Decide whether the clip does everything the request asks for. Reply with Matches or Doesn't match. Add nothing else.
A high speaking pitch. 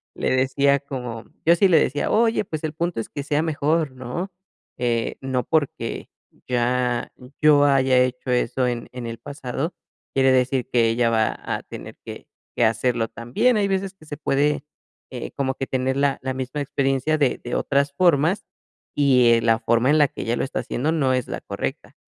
Doesn't match